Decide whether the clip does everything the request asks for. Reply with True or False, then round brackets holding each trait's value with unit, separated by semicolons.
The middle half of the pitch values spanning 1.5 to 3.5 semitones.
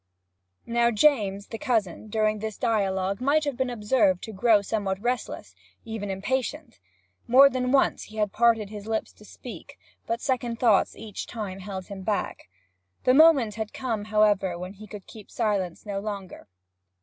True (3.1 semitones)